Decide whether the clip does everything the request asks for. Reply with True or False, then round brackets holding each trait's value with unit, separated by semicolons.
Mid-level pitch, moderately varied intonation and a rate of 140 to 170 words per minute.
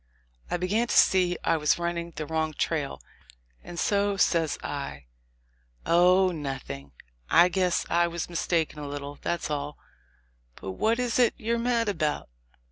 True (170 Hz; 4.0 semitones; 150 wpm)